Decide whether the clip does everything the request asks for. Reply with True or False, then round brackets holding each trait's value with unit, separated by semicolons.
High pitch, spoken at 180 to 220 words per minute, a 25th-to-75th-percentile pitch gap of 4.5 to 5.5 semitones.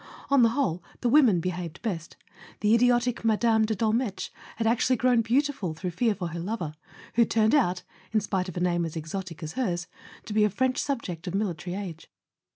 True (210 Hz; 205 wpm; 5.0 semitones)